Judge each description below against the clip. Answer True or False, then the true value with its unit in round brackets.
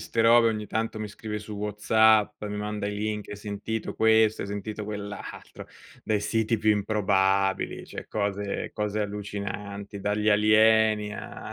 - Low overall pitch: True (105 Hz)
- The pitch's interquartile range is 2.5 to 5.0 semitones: False (1.1 semitones)